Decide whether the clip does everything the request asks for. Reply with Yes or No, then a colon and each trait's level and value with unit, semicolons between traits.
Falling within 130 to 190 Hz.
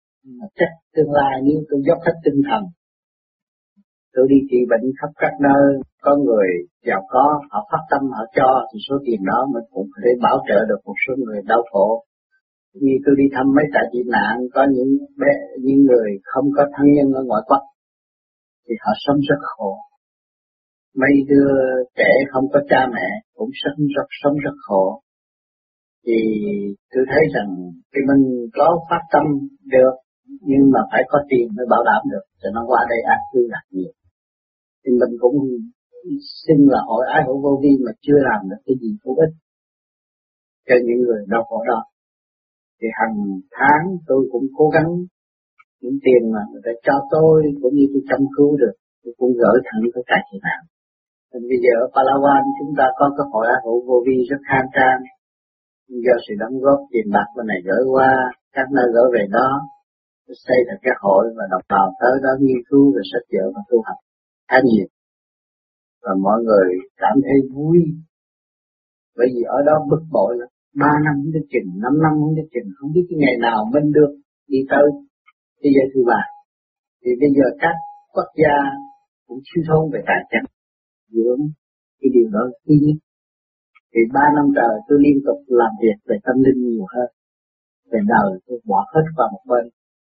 Yes: low, 135 Hz